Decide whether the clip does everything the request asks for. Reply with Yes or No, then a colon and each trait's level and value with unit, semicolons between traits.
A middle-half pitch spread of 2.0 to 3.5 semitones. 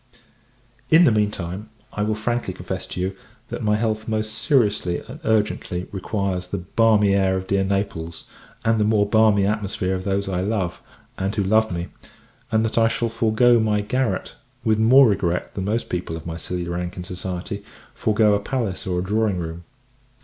Yes: average, 3.0 semitones